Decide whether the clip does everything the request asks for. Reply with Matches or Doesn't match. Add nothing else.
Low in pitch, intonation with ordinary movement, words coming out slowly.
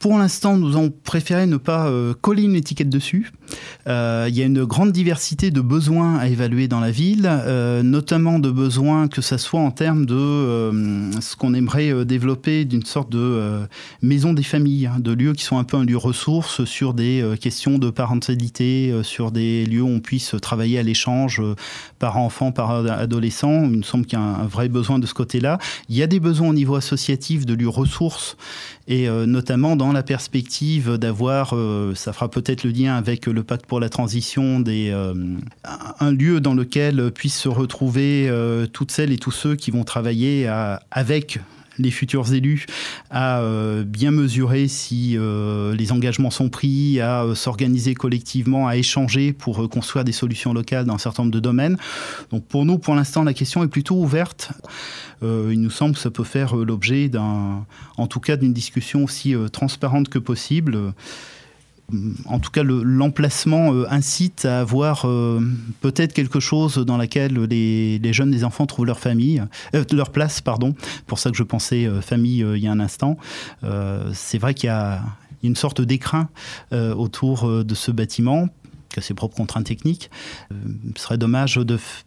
Doesn't match